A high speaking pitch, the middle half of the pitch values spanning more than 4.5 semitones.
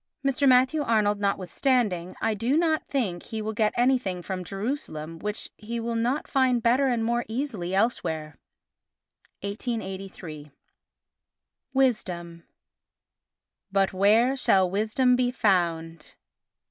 Yes: high, 220 Hz; average, 5.1 semitones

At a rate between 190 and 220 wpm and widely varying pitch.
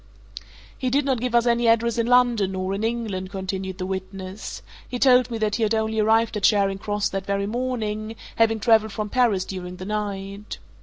No: average, 200 wpm; average, 3.0 semitones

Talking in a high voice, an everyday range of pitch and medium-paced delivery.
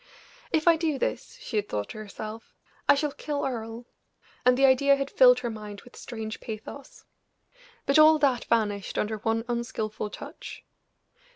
Yes: high, 240 Hz; average, 4.3 semitones; average, 165 wpm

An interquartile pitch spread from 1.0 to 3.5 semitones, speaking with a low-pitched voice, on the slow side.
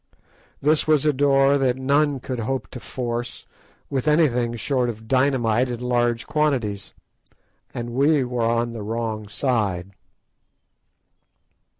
Yes: average, 2.9 semitones; low, 125 Hz; slow, 125 wpm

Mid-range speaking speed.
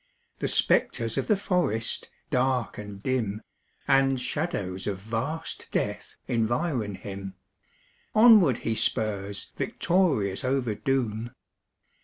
No: slow, 105 wpm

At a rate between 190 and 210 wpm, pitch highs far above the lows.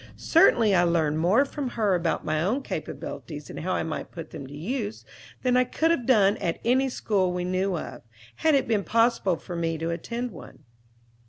Yes: average, 200 wpm; wide, 6.6 semitones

